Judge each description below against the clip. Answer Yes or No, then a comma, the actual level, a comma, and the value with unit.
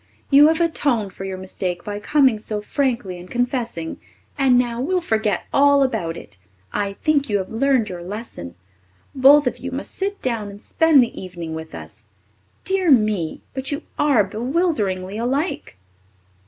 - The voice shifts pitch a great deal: Yes, wide, 6.4 semitones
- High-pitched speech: Yes, high, 235 Hz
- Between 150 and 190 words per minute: Yes, average, 170 wpm